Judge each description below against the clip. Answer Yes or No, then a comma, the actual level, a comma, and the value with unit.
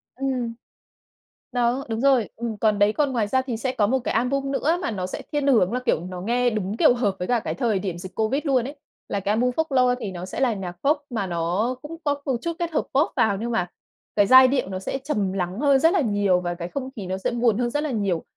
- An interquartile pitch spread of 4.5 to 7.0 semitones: Yes, average, 5.1 semitones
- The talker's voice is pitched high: Yes, high, 235 Hz